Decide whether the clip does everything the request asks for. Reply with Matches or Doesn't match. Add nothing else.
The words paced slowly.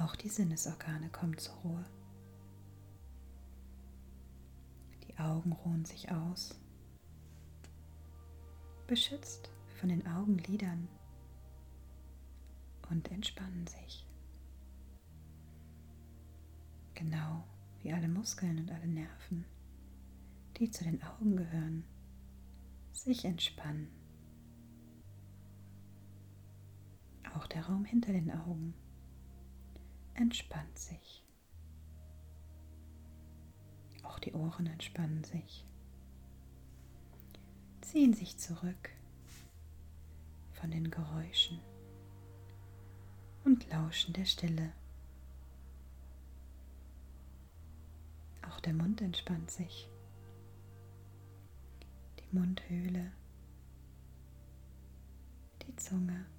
Matches